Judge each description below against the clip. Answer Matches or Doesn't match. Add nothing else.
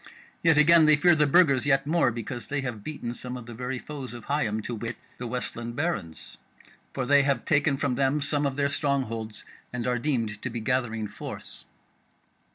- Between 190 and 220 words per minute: Matches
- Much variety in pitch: Doesn't match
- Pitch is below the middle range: Matches